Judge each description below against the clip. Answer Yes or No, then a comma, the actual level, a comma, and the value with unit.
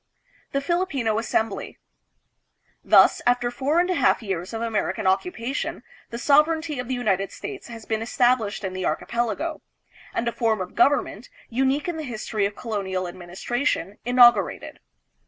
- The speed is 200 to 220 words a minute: No, average, 150 wpm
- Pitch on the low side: No, high, 235 Hz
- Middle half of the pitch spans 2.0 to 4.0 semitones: No, average, 5.0 semitones